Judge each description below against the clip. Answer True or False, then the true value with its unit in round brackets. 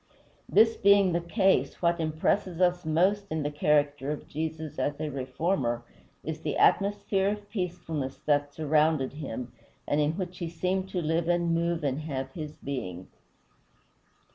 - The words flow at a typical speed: True (155 wpm)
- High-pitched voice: False (160 Hz)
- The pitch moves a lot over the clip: False (3.8 semitones)